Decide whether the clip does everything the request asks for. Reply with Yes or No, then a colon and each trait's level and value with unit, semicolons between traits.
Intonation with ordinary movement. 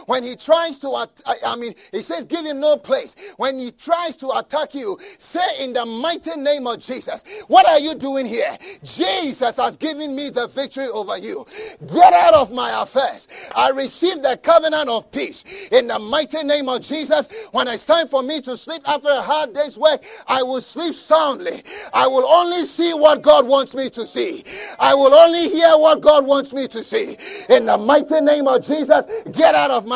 Yes: average, 3.8 semitones